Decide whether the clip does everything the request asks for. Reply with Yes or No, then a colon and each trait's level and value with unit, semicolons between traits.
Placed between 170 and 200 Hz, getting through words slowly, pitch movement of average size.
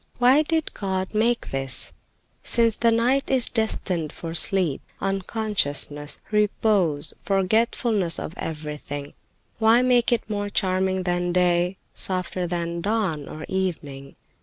Yes: high, 190 Hz; slow, 120 wpm; average, 4.9 semitones